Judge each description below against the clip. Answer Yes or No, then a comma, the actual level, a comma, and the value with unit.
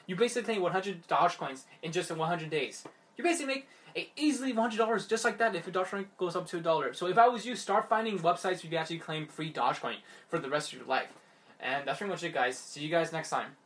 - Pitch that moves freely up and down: Yes, wide, 5.8 semitones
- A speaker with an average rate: No, fast, 285 wpm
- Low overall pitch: No, medium, 180 Hz